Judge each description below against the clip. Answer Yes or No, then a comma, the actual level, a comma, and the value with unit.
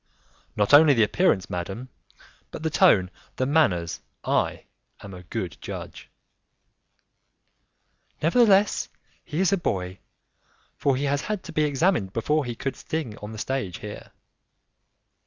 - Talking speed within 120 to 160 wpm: Yes, average, 140 wpm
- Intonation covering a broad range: Yes, wide, 7.7 semitones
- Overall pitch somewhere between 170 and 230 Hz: No, low, 135 Hz